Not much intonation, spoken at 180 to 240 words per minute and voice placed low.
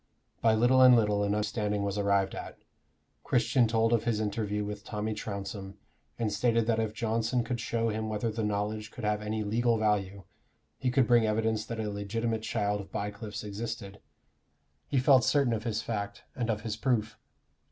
Yes: narrow, 1.9 semitones; average, 185 wpm; low, 110 Hz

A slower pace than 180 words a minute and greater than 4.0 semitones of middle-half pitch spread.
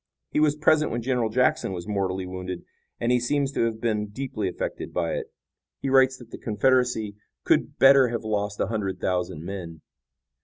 No: average, 185 wpm; average, 5.2 semitones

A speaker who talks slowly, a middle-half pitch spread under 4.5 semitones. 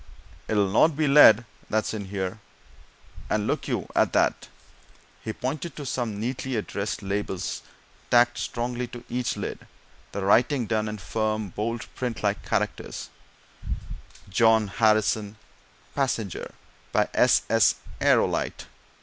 Yes: slow, 125 wpm; average, 3.0 semitones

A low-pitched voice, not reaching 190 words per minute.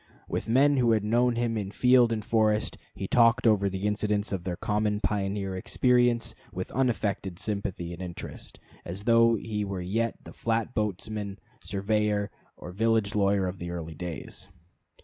Yes: low, 105 Hz; average, 165 wpm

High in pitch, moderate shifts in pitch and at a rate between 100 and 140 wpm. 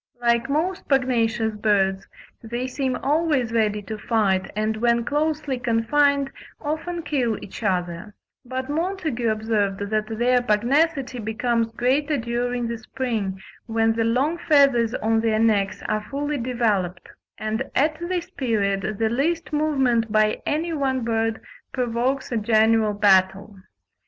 Yes: high, 235 Hz; average, 4.1 semitones; slow, 135 wpm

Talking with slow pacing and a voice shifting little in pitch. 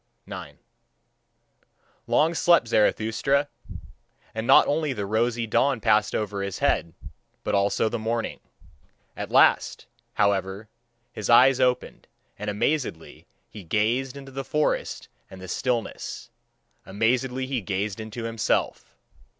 No: slow, 120 wpm; average, 4.1 semitones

